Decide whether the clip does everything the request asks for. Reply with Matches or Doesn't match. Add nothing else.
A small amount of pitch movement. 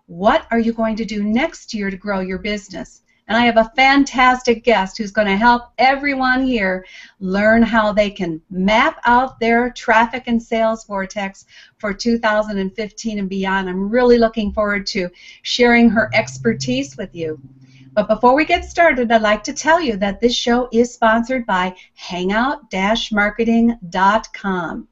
Doesn't match